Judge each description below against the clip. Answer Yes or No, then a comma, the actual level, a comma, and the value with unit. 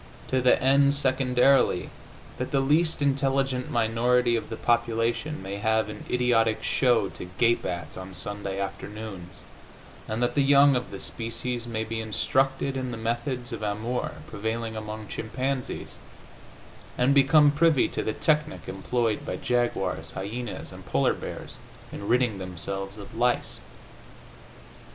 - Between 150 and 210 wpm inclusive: No, average, 140 wpm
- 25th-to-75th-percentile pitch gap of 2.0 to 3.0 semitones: No, average, 3.6 semitones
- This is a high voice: No, low, 120 Hz